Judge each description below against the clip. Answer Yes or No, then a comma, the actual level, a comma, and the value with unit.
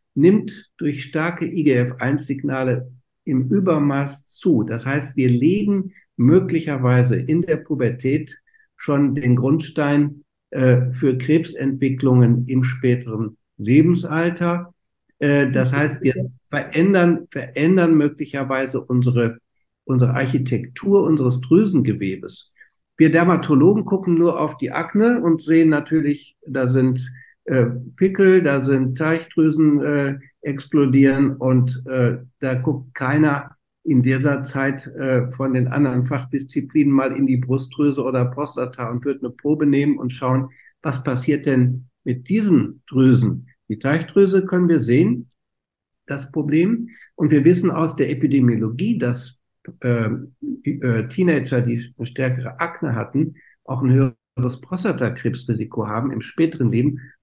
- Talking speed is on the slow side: Yes, slow, 120 wpm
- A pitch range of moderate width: Yes, average, 3.7 semitones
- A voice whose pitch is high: No, medium, 140 Hz